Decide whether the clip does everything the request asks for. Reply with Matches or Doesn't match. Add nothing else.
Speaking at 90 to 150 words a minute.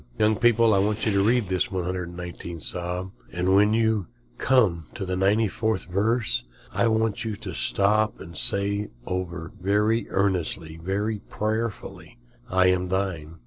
Matches